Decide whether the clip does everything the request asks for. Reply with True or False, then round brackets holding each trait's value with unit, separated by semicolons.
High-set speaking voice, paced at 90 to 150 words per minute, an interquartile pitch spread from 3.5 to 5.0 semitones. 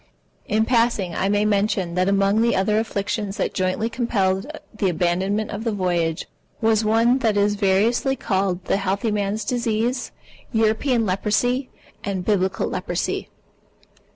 False (205 Hz; 140 wpm; 2.8 semitones)